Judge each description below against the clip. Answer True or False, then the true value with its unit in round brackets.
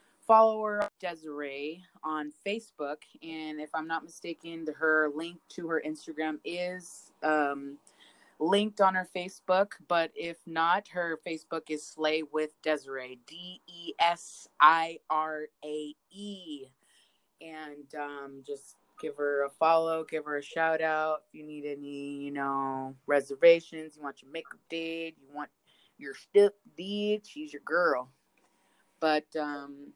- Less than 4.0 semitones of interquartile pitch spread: True (2.5 semitones)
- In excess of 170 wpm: False (140 wpm)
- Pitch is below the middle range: False (155 Hz)